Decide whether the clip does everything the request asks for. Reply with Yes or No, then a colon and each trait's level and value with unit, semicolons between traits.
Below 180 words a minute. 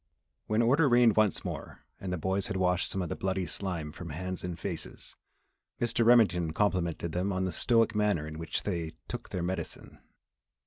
No: average, 185 wpm